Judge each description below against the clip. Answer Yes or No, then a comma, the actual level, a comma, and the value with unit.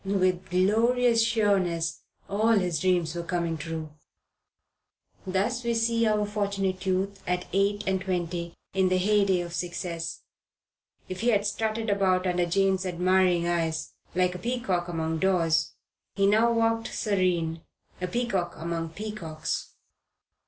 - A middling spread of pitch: Yes, average, 3.1 semitones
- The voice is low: No, medium, 185 Hz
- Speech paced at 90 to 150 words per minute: Yes, slow, 135 wpm